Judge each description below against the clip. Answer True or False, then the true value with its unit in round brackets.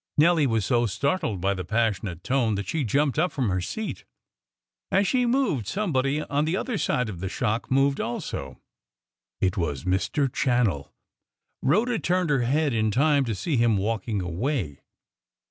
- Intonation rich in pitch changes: True (7.1 semitones)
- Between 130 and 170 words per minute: True (165 wpm)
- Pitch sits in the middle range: False (125 Hz)